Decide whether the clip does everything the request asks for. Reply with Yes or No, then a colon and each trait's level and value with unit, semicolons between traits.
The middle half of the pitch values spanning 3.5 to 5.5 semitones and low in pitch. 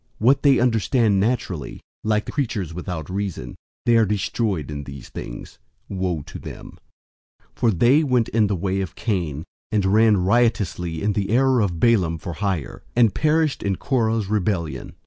Yes: average, 4.7 semitones; low, 100 Hz